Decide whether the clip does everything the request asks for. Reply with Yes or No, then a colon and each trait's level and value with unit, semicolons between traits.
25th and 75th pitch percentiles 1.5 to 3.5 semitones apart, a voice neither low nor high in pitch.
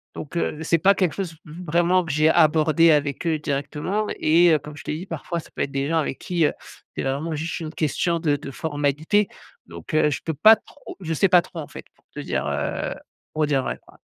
Yes: narrow, 2.5 semitones; medium, 155 Hz